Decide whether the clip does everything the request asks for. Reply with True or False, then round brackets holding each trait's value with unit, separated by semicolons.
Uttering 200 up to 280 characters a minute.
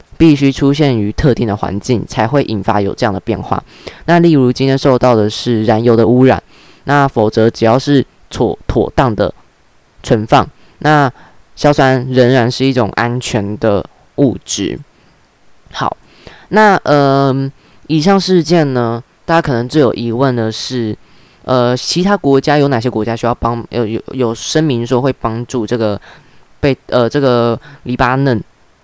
True (225 characters per minute)